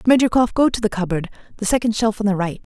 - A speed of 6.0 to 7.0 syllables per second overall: Yes, 6.7 syllables/s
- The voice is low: No, high, 215 Hz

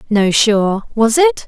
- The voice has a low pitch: No, high, 220 Hz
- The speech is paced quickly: No, average, 165 wpm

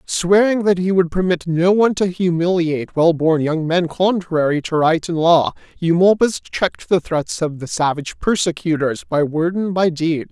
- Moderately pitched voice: Yes, medium, 170 Hz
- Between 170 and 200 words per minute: Yes, average, 180 wpm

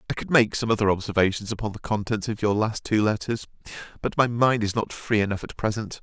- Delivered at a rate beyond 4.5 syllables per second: Yes, 6.1 syllables/s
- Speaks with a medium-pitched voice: No, low, 105 Hz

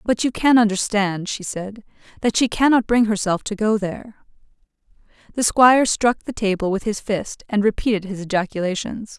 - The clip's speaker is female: Yes, female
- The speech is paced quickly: No, average, 170 wpm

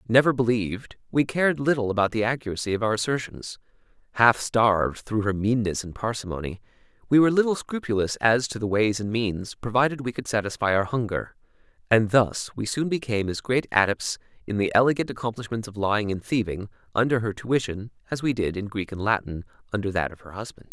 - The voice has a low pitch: Yes, low, 115 Hz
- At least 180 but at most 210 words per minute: Yes, average, 190 wpm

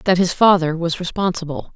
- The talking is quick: No, average, 170 wpm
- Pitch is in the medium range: Yes, medium, 175 Hz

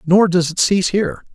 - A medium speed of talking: No, fast, 225 wpm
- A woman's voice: No, male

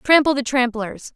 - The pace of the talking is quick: No, average, 155 wpm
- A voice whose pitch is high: Yes, very high, 255 Hz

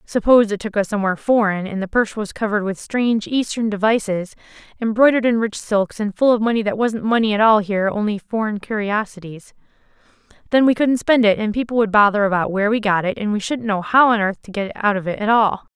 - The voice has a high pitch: Yes, high, 215 Hz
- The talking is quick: Yes, fast, 230 wpm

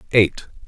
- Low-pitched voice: Yes, low, 105 Hz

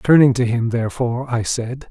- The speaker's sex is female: No, male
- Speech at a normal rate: Yes, average, 190 wpm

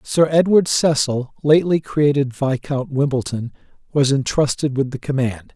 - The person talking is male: Yes, male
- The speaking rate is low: Yes, slow, 130 wpm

